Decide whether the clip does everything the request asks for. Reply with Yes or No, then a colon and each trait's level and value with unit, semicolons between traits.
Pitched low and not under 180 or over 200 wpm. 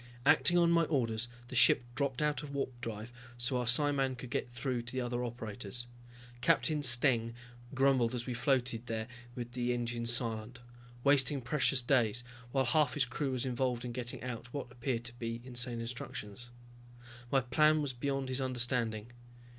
No: low, 125 Hz; average, 170 wpm